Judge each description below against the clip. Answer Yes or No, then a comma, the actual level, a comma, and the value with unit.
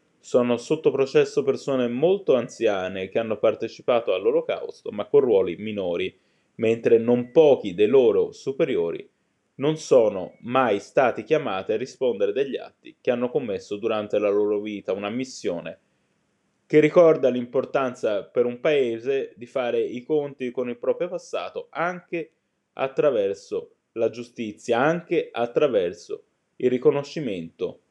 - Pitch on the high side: Yes, very high, 390 Hz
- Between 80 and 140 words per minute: Yes, average, 130 wpm